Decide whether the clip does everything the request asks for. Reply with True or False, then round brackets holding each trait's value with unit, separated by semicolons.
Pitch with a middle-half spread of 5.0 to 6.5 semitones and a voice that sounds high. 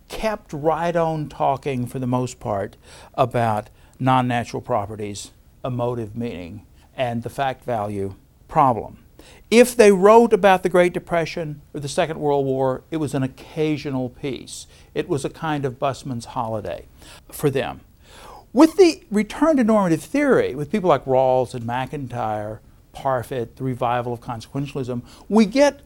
False (5.5 semitones; 135 Hz)